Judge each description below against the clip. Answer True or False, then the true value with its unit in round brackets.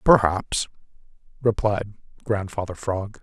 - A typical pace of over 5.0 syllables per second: False (3.8 syllables/s)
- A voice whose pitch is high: False (100 Hz)